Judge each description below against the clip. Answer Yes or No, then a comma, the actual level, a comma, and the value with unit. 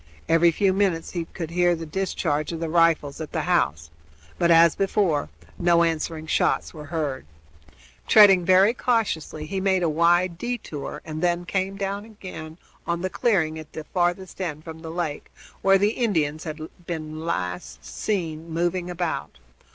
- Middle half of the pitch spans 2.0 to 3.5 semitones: Yes, average, 3.0 semitones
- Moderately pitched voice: Yes, medium, 170 Hz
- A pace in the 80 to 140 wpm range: No, average, 165 wpm